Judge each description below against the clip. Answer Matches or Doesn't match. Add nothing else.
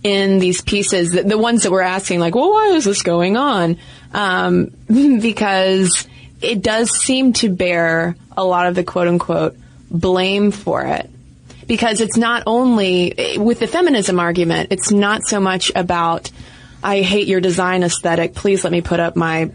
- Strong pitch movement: Doesn't match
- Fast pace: Doesn't match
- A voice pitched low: Doesn't match